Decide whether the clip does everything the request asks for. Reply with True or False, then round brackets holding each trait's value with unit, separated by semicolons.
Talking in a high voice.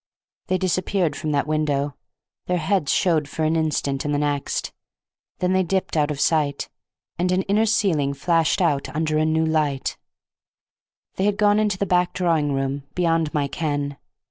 False (160 Hz)